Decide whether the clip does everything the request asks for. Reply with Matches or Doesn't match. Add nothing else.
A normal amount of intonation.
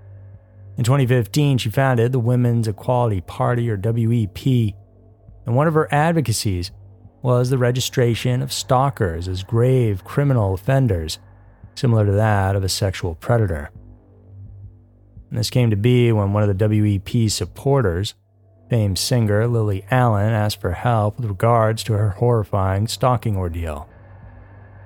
Matches